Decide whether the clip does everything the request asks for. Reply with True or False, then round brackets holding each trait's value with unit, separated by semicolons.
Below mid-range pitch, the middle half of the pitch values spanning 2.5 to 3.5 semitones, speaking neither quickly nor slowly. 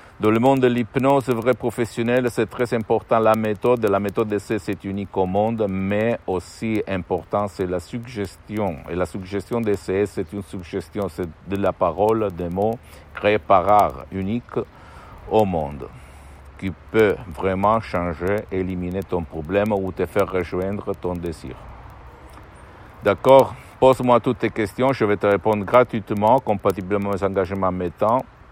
True (100 Hz; 3.0 semitones; 150 wpm)